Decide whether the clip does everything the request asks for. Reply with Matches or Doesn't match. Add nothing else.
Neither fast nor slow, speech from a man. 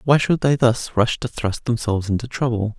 Doesn't match